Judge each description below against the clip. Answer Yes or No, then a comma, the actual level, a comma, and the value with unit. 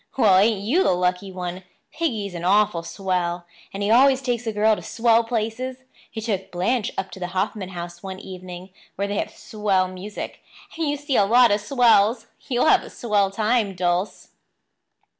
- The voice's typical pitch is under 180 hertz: No, high, 205 Hz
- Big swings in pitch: No, average, 3.9 semitones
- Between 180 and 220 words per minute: Yes, average, 185 wpm